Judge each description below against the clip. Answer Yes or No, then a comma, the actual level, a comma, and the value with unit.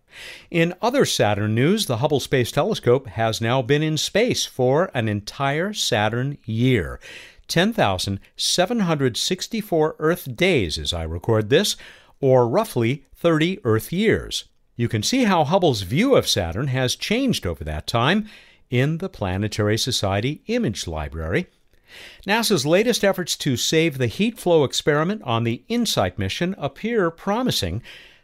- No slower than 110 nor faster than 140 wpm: Yes, slow, 135 wpm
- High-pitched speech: No, low, 135 Hz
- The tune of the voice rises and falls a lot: Yes, wide, 8.5 semitones